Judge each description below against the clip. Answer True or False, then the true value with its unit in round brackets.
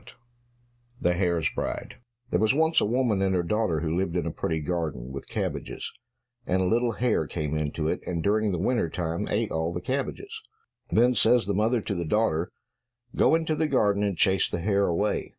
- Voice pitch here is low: True (95 Hz)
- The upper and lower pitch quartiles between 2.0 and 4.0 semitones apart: False (5.2 semitones)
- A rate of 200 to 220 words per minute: True (205 wpm)